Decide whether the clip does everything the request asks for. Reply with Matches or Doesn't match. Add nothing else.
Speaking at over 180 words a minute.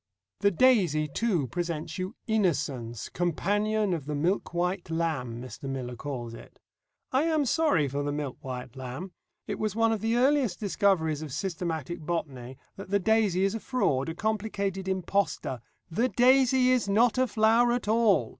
Doesn't match